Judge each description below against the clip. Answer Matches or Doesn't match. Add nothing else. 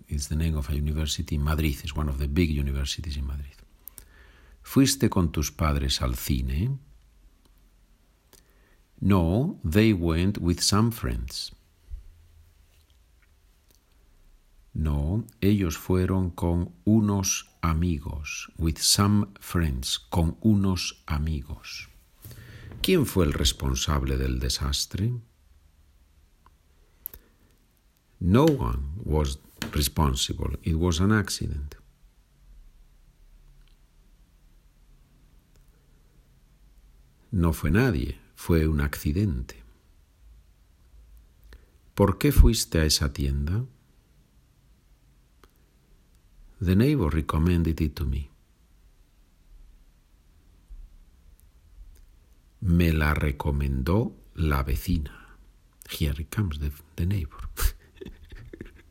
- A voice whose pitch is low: Matches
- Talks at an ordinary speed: Doesn't match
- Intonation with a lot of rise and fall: Doesn't match